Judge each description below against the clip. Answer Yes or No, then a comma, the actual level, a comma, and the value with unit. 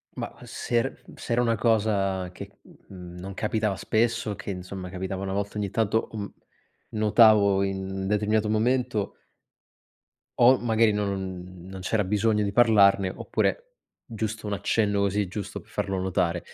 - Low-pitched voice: Yes, low, 100 Hz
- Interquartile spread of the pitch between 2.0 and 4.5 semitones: Yes, narrow, 2.4 semitones